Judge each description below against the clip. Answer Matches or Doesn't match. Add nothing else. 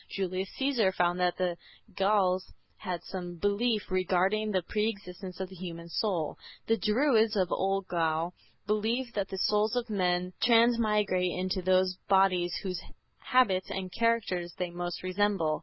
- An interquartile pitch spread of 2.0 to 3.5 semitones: Matches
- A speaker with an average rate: Matches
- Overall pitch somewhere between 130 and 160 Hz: Doesn't match